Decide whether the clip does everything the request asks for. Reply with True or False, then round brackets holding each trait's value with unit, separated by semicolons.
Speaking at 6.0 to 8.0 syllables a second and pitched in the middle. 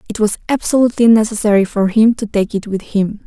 False (6.2 syllables/s; 215 Hz)